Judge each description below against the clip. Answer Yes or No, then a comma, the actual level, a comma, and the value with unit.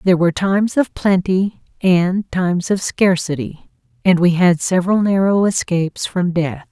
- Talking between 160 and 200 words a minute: No, average, 150 wpm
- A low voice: No, medium, 180 Hz